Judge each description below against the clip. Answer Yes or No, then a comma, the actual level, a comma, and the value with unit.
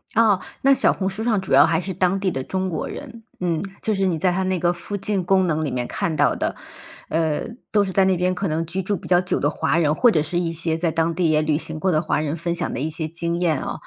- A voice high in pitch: No, medium, 175 Hz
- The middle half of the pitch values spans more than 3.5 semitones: No, average, 3.1 semitones